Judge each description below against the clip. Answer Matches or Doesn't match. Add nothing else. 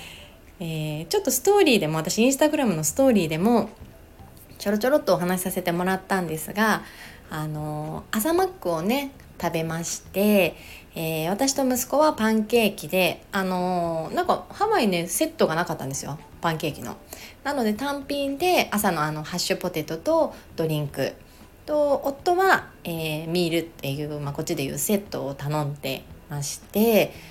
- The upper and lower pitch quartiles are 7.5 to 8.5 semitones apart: Matches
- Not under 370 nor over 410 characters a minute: Doesn't match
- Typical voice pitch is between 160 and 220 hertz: Matches